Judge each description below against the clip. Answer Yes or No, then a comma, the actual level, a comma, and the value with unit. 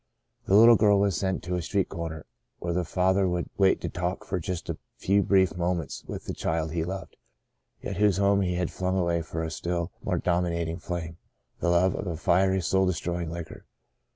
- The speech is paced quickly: Yes, fast, 210 wpm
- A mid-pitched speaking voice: No, very low, 90 Hz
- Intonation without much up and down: Yes, narrow, 2.0 semitones